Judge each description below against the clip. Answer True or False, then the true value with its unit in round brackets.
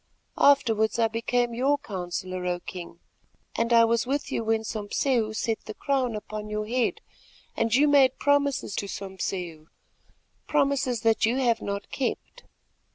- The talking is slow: False (145 wpm)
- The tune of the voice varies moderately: True (3.7 semitones)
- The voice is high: True (230 Hz)